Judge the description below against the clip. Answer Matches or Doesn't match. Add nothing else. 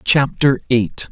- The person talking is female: Doesn't match